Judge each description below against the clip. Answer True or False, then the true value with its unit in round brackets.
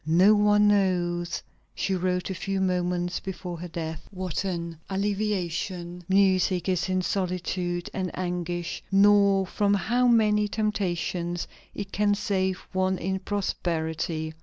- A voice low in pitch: False (185 Hz)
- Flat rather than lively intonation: True (2.3 semitones)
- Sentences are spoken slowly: True (130 wpm)